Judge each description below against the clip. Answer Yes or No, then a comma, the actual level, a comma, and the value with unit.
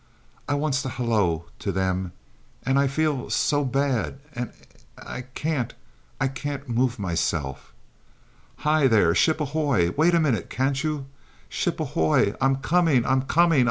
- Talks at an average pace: Yes, average, 150 wpm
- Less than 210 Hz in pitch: Yes, low, 135 Hz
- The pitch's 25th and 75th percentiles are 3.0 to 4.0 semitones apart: No, average, 4.8 semitones